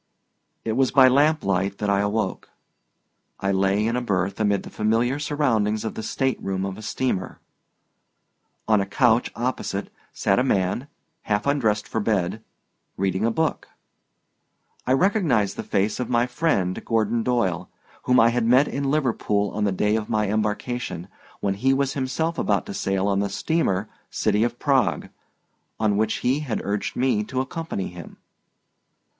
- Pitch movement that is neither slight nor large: Yes, average, 4.5 semitones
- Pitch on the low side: Yes, low, 110 Hz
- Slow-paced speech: No, average, 160 wpm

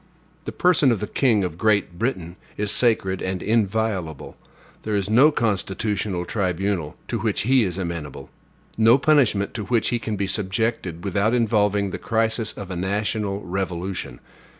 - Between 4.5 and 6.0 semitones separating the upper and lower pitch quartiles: No, average, 3.2 semitones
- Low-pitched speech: Yes, low, 100 Hz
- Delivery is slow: No, average, 155 wpm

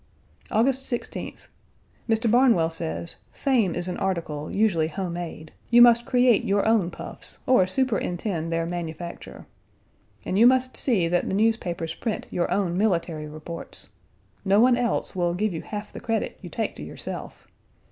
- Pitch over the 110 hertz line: Yes, high, 190 Hz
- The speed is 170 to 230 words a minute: No, average, 155 wpm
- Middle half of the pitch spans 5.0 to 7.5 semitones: Yes, wide, 5.4 semitones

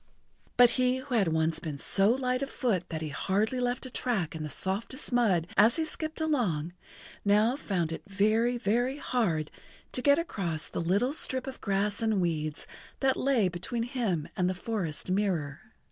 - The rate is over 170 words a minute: Yes, average, 180 wpm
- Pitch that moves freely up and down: Yes, wide, 6.3 semitones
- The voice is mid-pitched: No, high, 210 Hz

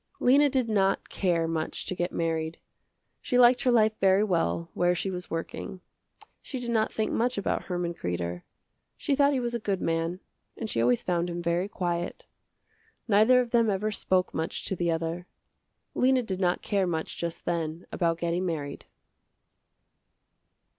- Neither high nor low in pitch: Yes, medium, 180 Hz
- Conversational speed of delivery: Yes, average, 170 wpm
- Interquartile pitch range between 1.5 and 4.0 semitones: No, average, 4.6 semitones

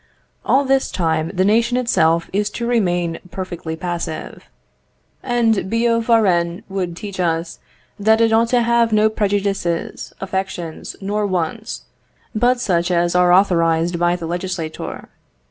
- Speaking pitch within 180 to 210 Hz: Yes, high, 190 Hz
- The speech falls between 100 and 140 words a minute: Yes, slow, 135 wpm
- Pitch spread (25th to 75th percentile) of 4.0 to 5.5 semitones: Yes, average, 4.6 semitones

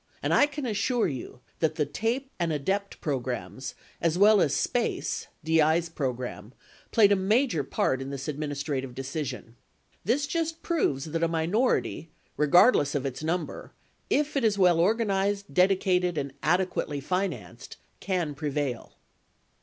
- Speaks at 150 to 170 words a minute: No, average, 140 wpm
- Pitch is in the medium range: Yes, medium, 170 Hz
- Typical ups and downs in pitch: No, wide, 6.3 semitones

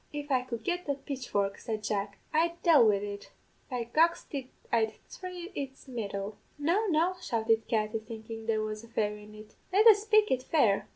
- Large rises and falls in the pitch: Yes, wide, 6.6 semitones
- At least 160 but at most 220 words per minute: Yes, average, 185 wpm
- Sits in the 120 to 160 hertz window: No, high, 235 Hz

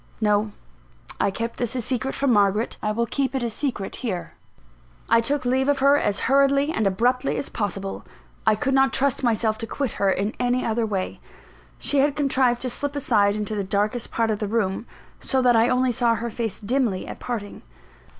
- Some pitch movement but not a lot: Yes, average, 3.9 semitones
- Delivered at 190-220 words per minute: Yes, average, 200 wpm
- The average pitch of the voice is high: Yes, high, 235 Hz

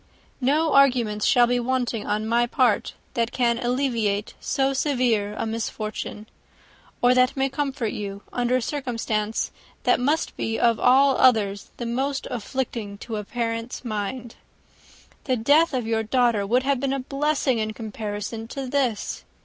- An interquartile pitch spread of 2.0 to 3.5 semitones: Yes, average, 3.2 semitones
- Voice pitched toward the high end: Yes, high, 240 Hz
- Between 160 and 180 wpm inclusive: No, average, 150 wpm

